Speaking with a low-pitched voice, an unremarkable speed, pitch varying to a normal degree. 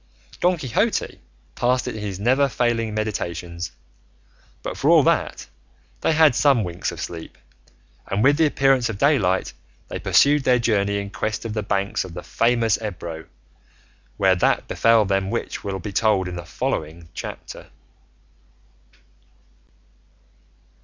Yes: low, 110 Hz; average, 145 wpm; average, 4.8 semitones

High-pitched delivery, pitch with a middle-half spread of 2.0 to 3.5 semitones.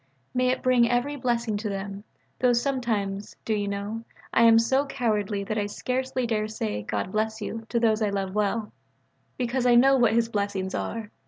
Yes: high, 225 Hz; average, 3.1 semitones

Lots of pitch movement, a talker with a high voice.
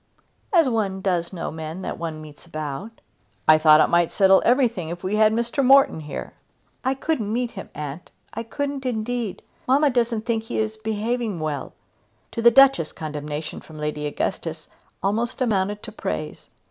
Yes: wide, 6.9 semitones; high, 210 Hz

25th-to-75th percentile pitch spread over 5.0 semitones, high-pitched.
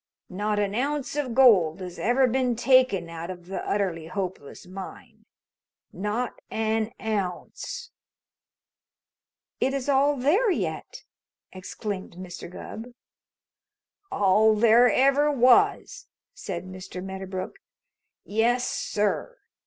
Yes: wide, 5.6 semitones; high, 215 Hz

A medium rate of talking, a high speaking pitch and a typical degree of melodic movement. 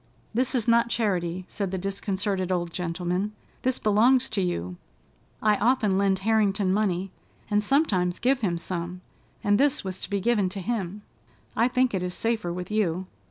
Yes: average, 170 wpm; high, 200 Hz; average, 3.6 semitones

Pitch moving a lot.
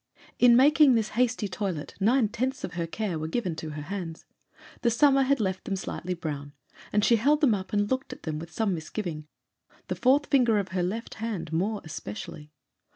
Yes: wide, 6.4 semitones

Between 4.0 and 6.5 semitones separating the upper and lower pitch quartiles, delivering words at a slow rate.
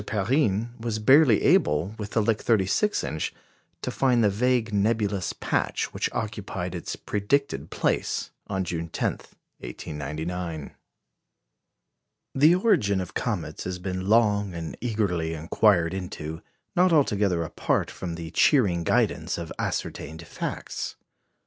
Yes: average, 4.9 semitones; slow, 125 wpm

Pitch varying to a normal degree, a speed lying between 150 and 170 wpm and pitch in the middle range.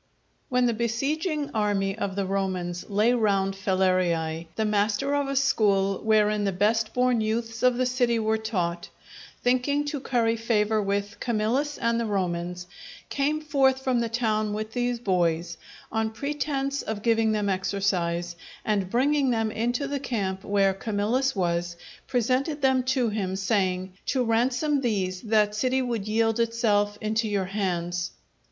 No: average, 4.2 semitones; average, 155 wpm; high, 220 Hz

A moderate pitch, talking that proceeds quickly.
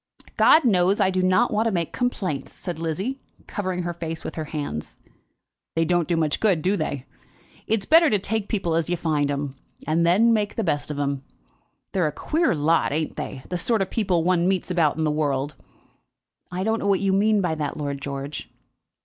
Yes: medium, 175 Hz; fast, 210 wpm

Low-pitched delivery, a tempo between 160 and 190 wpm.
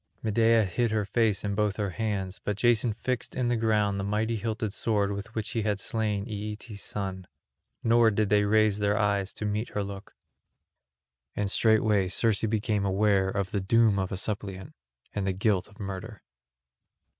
Yes: low, 105 Hz; average, 180 wpm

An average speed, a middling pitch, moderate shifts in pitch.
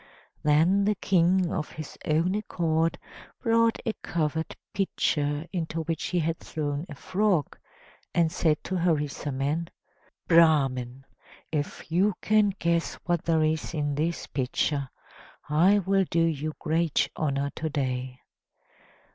No: slow, 130 wpm; medium, 160 Hz; average, 3.1 semitones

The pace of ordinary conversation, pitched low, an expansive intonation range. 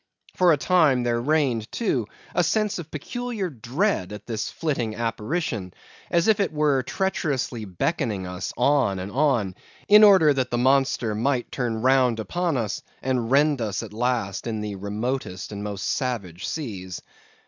Yes: average, 160 wpm; low, 125 Hz; wide, 6.2 semitones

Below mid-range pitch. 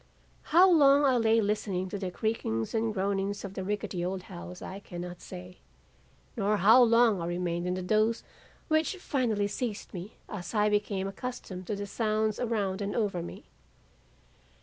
No: high, 205 Hz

